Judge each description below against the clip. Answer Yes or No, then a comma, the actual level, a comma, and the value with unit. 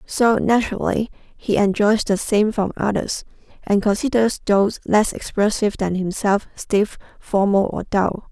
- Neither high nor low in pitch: No, high, 205 Hz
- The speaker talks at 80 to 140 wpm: Yes, slow, 135 wpm